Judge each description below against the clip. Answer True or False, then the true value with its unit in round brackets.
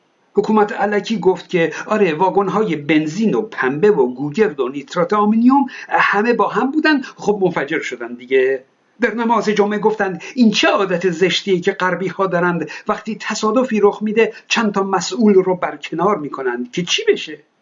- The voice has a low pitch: False (200 Hz)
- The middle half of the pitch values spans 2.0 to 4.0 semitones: True (3.5 semitones)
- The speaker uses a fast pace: True (160 wpm)